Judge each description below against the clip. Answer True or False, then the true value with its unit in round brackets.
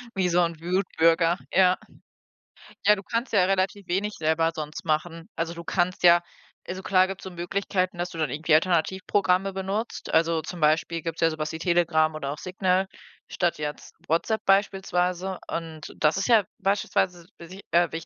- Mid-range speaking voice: True (175 Hz)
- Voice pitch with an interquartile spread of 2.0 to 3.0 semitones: True (2.6 semitones)